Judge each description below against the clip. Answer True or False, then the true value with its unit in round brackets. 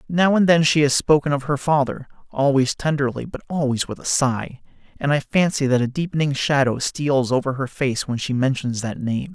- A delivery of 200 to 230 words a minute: True (205 wpm)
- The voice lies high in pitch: False (140 Hz)